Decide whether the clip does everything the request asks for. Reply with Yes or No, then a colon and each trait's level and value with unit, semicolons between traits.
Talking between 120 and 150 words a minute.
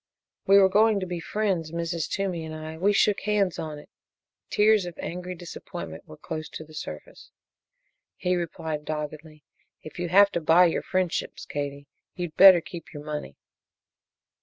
No: average, 165 wpm